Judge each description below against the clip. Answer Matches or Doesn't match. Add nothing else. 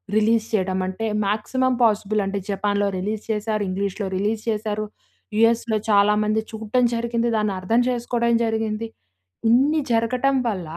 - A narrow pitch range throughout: Matches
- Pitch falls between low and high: Doesn't match